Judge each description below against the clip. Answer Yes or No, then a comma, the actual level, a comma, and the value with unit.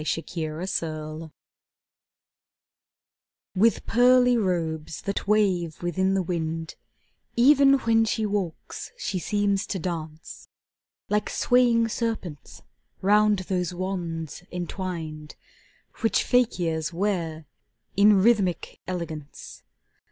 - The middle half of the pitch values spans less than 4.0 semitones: No, average, 4.5 semitones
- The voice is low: No, medium, 185 Hz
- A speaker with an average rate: No, slow, 90 wpm